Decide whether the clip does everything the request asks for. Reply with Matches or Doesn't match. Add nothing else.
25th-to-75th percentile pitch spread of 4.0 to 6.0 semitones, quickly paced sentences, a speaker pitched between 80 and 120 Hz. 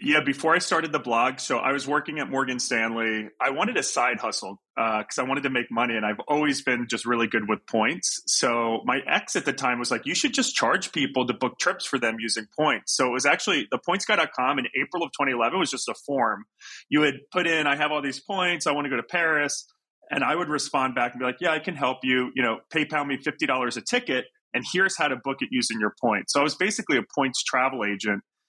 Doesn't match